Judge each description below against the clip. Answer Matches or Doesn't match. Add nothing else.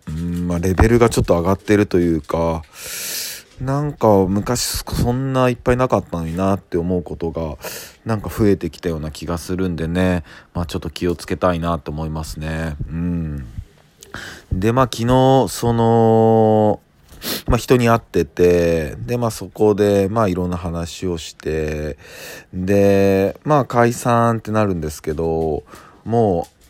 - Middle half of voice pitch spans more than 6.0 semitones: Doesn't match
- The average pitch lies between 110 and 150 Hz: Doesn't match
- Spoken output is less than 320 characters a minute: Matches